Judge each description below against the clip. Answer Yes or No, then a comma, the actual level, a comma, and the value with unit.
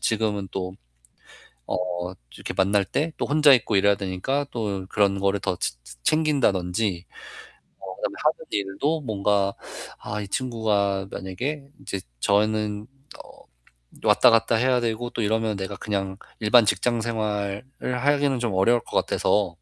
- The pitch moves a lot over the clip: No, average, 3.5 semitones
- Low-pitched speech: Yes, low, 105 Hz